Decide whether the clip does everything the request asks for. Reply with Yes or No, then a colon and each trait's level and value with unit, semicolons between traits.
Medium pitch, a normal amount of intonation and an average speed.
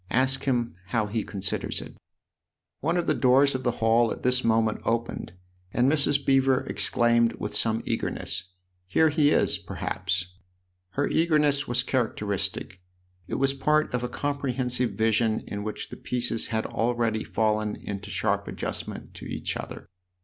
No: low, 120 Hz; average, 3.8 semitones; average, 160 wpm